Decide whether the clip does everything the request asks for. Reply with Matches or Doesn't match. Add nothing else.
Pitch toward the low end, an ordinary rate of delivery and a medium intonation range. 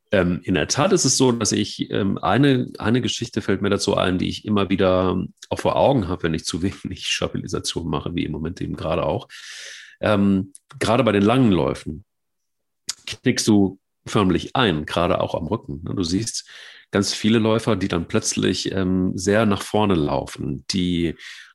Matches